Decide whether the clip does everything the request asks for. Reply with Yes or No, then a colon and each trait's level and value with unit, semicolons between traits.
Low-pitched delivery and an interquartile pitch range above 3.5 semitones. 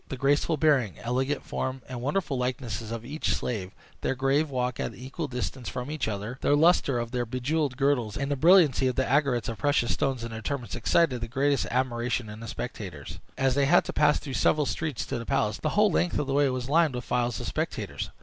No: low, 130 Hz; average, 3.1 semitones